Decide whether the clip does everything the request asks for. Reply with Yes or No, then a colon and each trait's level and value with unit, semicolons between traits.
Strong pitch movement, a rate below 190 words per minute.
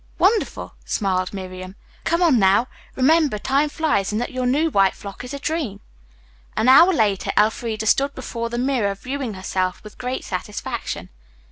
Yes: wide, 5.9 semitones; average, 160 wpm